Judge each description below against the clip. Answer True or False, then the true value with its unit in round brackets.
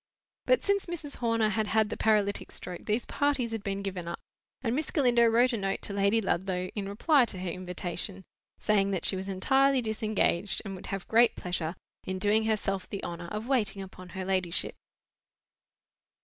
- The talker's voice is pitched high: True (205 Hz)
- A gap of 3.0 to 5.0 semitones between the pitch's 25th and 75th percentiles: True (3.4 semitones)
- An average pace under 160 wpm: False (185 wpm)